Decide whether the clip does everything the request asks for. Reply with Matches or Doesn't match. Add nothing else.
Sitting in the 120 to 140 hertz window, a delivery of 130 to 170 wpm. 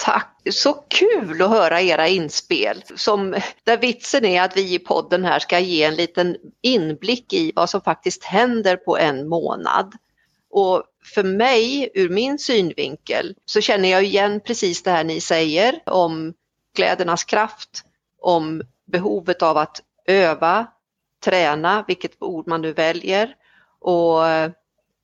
Doesn't match